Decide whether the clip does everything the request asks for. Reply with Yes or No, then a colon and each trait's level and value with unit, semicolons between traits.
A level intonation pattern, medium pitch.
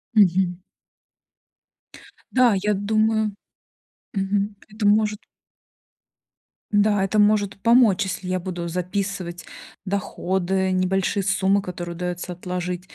No: narrow, 2.3 semitones; high, 195 Hz